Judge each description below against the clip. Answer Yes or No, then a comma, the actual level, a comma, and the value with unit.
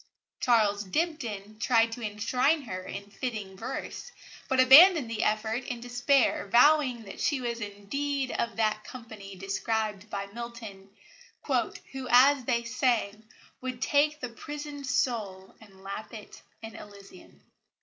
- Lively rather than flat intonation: No, average, 3.9 semitones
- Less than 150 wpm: Yes, slow, 135 wpm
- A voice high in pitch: Yes, high, 230 Hz